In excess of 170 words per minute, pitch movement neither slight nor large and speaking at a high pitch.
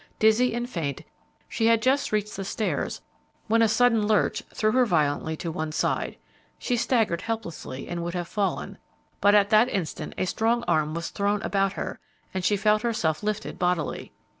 Yes: average, 180 wpm; average, 4.7 semitones; high, 210 Hz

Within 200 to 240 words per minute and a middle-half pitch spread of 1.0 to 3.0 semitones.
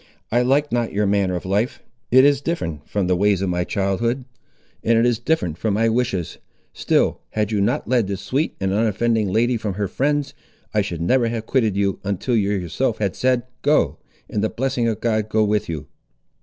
No: fast, 205 wpm; average, 3.6 semitones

